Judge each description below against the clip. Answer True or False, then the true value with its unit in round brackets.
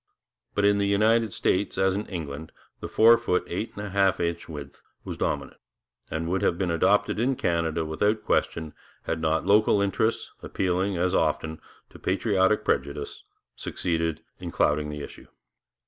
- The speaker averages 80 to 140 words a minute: False (165 wpm)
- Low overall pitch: True (90 Hz)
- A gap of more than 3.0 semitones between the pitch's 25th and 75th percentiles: True (4.1 semitones)